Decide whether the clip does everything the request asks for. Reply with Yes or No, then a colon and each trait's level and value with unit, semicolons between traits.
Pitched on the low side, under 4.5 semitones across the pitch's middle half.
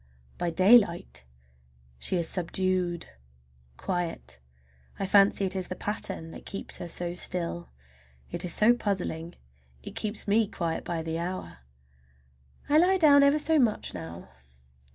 No: medium, 185 Hz; average, 3.7 semitones